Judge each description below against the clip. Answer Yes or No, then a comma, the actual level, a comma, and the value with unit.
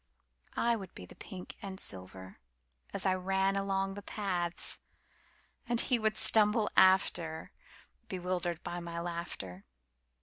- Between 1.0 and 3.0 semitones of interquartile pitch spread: Yes, narrow, 2.6 semitones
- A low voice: No, medium, 185 Hz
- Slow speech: Yes, slow, 115 wpm